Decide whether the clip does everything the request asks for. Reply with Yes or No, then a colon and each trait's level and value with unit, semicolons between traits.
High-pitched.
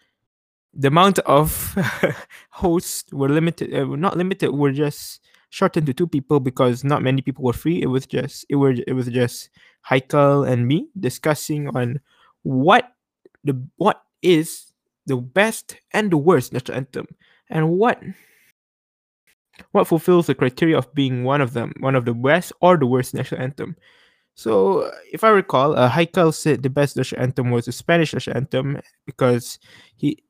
No: medium, 140 Hz